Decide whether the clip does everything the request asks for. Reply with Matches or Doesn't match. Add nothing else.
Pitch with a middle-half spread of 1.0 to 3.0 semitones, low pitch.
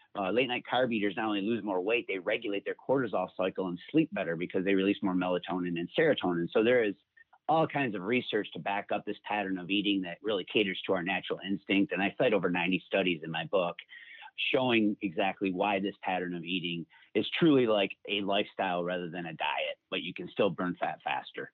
Matches